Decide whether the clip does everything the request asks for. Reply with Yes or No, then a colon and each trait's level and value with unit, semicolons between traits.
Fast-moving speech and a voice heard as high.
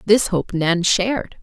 No: average, 170 wpm; high, 195 Hz